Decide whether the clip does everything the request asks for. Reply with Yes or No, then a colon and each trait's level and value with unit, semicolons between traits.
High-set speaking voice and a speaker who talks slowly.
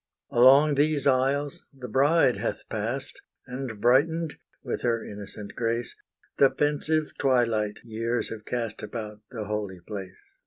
No: low, 120 Hz; slow, 130 wpm